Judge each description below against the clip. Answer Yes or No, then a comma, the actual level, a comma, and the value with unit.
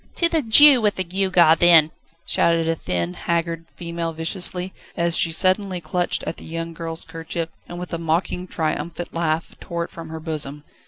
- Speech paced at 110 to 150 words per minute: No, average, 180 wpm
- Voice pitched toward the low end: No, medium, 170 Hz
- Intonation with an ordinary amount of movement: No, narrow, 1.6 semitones